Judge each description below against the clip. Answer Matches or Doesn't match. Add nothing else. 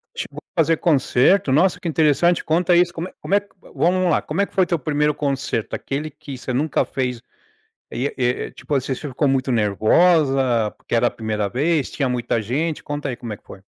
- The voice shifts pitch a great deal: Doesn't match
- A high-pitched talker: Doesn't match